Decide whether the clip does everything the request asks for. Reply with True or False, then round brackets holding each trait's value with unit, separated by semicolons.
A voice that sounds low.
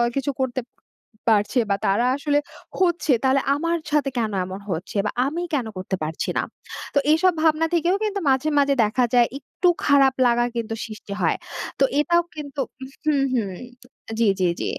False (275 Hz)